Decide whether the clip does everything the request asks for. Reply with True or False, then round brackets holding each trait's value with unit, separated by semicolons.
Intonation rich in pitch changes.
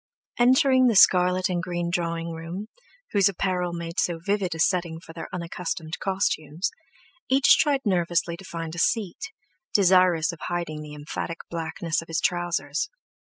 False (2.4 semitones)